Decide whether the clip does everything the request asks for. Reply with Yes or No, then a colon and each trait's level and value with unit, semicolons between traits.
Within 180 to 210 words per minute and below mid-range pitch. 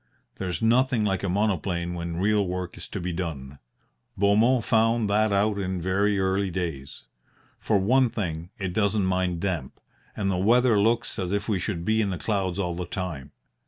Yes: average, 185 wpm; very low, 95 Hz